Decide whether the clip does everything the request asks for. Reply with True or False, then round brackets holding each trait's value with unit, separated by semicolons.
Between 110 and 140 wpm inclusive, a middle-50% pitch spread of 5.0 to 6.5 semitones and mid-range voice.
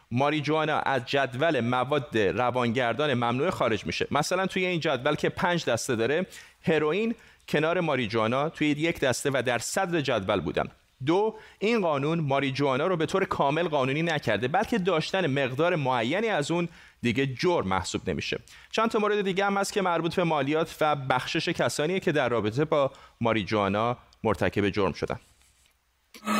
False (155 wpm; 5.6 semitones; 150 Hz)